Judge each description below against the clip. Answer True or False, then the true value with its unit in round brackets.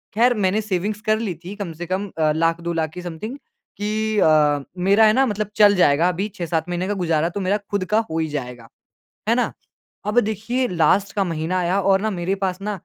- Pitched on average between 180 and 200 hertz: True (185 Hz)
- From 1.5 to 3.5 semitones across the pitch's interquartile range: False (4.0 semitones)